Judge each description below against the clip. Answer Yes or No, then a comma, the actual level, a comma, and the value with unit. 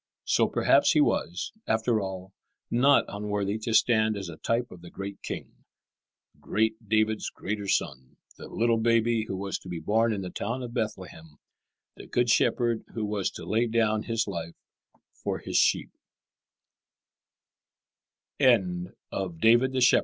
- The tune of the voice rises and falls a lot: No, average, 3.0 semitones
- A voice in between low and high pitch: No, low, 110 Hz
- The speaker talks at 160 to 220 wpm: No, average, 140 wpm